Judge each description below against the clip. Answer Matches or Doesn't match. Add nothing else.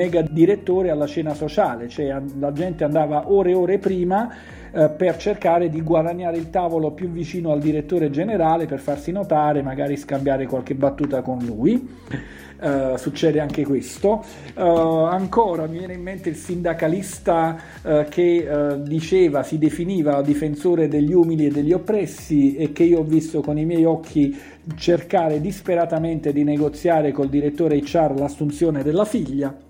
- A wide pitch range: Doesn't match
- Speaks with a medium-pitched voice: Matches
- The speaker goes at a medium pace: Matches